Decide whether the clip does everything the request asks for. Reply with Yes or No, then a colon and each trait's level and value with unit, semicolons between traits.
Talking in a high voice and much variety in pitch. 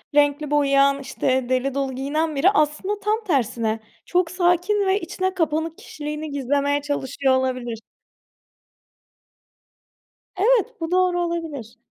No: very high, 295 Hz; average, 4.6 semitones